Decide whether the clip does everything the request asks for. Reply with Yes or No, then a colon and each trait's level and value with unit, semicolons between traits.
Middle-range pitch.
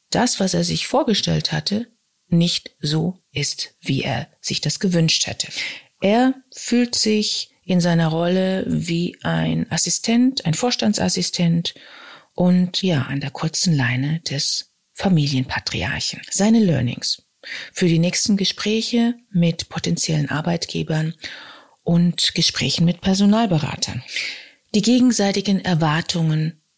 Yes: medium, 175 Hz